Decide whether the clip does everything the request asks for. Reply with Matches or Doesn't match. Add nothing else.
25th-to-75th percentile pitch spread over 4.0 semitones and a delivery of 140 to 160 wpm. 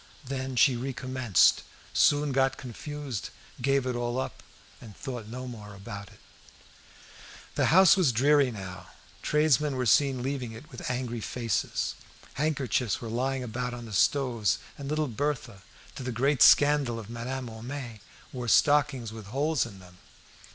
Doesn't match